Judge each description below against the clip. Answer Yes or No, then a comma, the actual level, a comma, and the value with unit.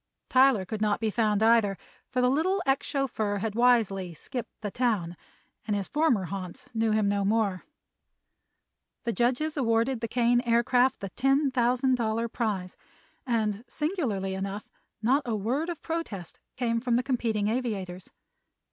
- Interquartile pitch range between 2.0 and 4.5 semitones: Yes, average, 3.8 semitones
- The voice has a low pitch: No, high, 230 Hz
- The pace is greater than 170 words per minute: No, average, 155 wpm